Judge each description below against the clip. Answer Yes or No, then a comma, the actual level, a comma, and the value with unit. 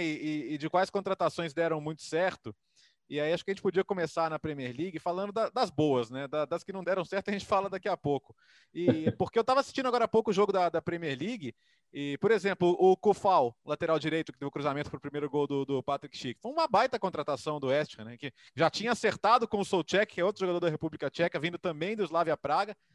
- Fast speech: Yes, fast, 250 wpm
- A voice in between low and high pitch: Yes, medium, 170 Hz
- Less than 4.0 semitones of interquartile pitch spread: No, average, 4.7 semitones